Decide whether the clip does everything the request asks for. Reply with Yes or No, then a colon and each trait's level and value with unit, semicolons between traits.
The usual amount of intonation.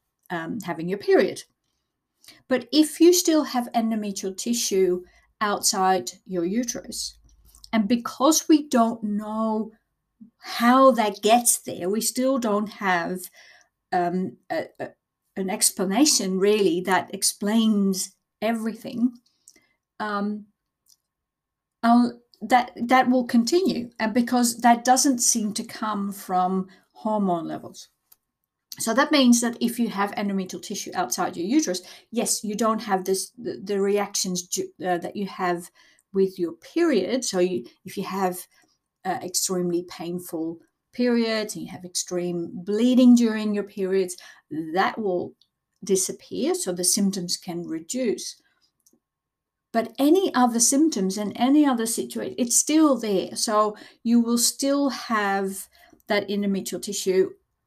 Yes: average, 4.4 semitones